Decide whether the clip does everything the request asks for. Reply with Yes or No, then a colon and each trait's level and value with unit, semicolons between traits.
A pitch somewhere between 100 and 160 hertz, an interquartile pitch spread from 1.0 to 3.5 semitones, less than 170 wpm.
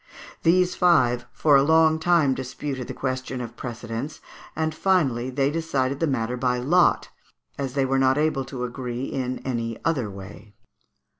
No: low, 135 Hz; average, 4.1 semitones; average, 160 wpm